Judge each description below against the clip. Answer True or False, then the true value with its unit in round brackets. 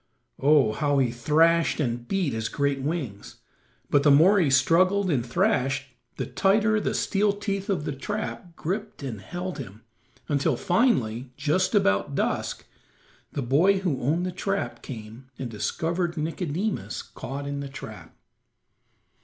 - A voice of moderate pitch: True (150 Hz)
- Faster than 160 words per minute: False (145 wpm)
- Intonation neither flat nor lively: False (5.8 semitones)